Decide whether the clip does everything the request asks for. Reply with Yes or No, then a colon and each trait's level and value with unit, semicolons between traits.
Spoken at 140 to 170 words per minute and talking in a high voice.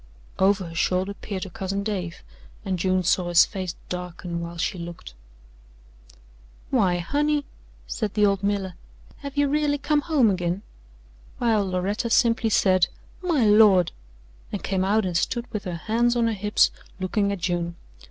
Yes: average, 160 wpm; high, 195 Hz